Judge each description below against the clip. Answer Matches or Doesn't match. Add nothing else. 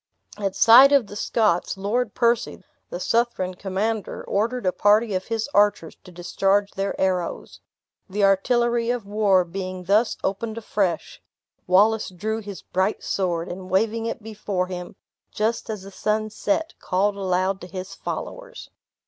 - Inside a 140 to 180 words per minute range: Matches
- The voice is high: Matches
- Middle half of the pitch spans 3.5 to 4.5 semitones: Doesn't match